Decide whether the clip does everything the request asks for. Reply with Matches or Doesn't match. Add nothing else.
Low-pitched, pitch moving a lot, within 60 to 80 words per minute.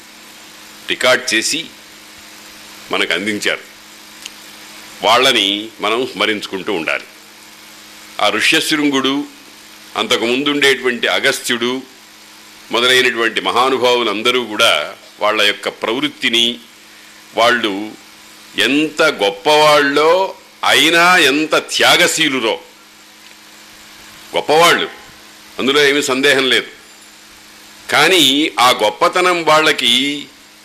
Matches